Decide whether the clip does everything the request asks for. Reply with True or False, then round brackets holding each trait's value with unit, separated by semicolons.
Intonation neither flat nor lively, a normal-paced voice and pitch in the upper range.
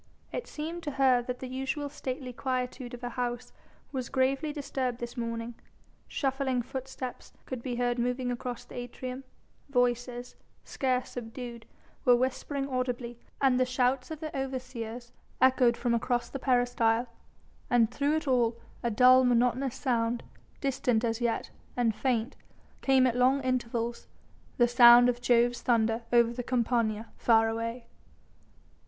False (1.5 semitones; 145 wpm; 245 Hz)